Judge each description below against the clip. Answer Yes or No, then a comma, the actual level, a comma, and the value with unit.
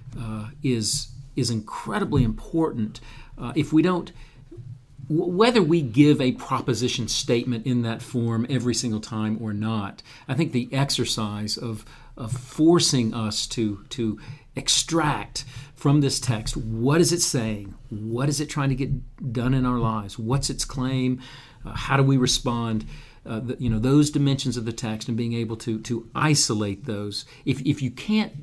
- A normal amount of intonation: Yes, average, 3.3 semitones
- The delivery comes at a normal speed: Yes, average, 170 wpm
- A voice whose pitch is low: Yes, low, 125 Hz